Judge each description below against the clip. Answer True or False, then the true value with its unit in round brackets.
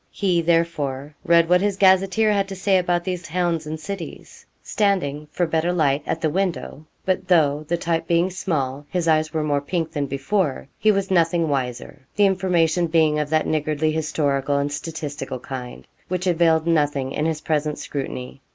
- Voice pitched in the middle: True (160 Hz)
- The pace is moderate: True (180 wpm)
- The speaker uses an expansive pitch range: False (3.5 semitones)